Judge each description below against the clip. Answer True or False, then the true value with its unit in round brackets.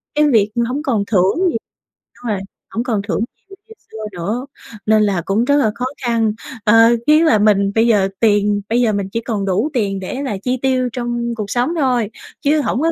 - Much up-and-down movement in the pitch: False (3.8 semitones)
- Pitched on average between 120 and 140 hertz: False (225 Hz)